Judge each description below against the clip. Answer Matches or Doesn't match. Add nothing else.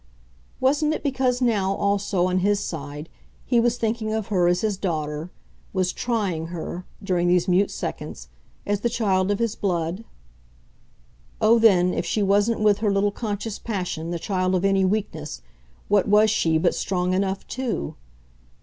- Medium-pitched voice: Doesn't match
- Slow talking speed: Doesn't match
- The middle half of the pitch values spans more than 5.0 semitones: Doesn't match